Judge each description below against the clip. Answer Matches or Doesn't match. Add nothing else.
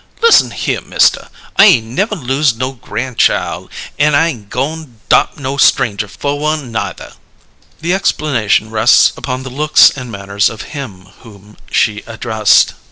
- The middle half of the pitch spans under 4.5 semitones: Doesn't match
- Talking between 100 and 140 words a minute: Doesn't match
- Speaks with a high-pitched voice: Doesn't match